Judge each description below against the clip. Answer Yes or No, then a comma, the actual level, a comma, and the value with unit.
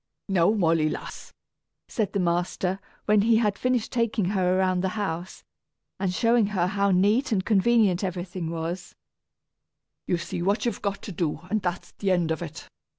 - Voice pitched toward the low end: No, high, 190 Hz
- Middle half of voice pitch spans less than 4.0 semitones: Yes, average, 3.1 semitones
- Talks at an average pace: Yes, average, 170 wpm